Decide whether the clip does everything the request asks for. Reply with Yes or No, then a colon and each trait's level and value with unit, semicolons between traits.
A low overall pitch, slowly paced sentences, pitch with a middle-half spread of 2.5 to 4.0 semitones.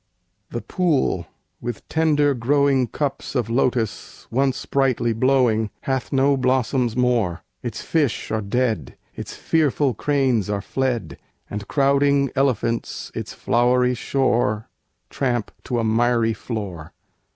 Yes: low, 125 Hz; slow, 120 wpm; average, 3.4 semitones